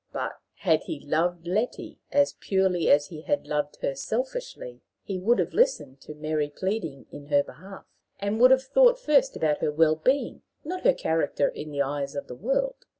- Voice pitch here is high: No, medium, 180 Hz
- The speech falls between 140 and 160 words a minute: No, average, 195 wpm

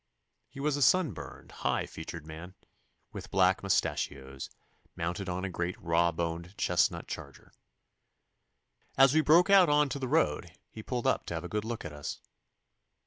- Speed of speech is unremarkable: Yes, average, 170 wpm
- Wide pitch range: Yes, wide, 8.4 semitones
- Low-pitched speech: Yes, very low, 95 Hz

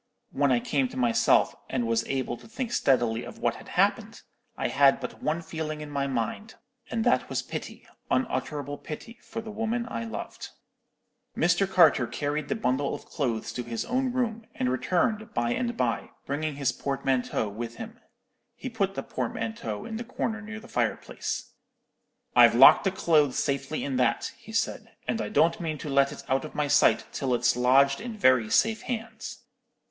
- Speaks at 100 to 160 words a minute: No, average, 185 wpm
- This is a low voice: No, medium, 145 Hz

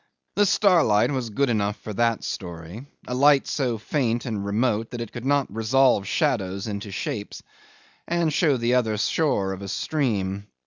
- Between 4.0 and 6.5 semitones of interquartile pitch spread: Yes, average, 4.9 semitones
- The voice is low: Yes, low, 115 Hz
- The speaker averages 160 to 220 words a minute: Yes, average, 165 wpm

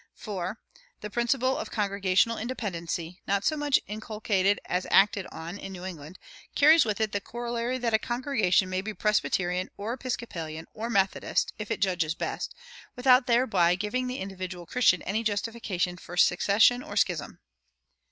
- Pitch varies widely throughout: No, average, 4.4 semitones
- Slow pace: No, average, 155 wpm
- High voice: Yes, high, 205 Hz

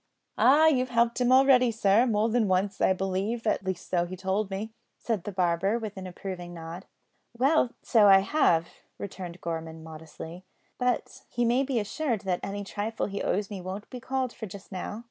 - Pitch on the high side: Yes, high, 200 Hz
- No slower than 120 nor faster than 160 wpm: No, average, 190 wpm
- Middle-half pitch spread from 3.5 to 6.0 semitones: Yes, average, 4.3 semitones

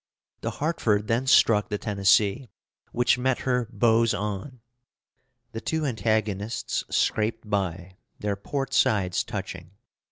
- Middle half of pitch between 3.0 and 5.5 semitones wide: Yes, average, 3.4 semitones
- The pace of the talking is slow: Yes, slow, 120 wpm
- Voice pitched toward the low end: Yes, low, 110 Hz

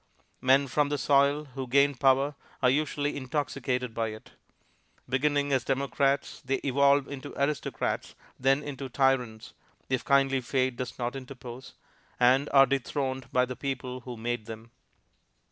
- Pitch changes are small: Yes, narrow, 1.9 semitones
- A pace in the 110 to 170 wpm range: Yes, average, 145 wpm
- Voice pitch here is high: No, low, 135 Hz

